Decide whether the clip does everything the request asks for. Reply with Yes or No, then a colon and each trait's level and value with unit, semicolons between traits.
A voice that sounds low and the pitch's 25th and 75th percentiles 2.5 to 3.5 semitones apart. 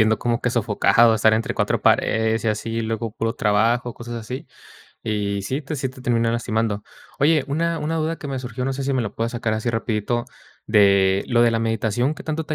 Yes: low, 115 Hz; average, 2.8 semitones